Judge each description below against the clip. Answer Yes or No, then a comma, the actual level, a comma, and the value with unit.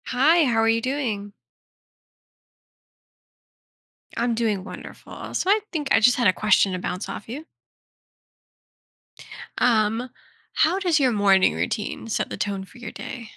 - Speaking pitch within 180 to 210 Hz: No, high, 230 Hz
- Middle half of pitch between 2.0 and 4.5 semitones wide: Yes, average, 4.2 semitones